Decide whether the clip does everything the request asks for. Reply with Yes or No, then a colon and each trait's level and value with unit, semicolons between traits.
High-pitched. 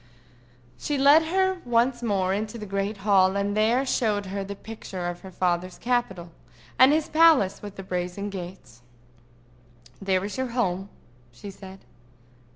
Yes: high, 200 Hz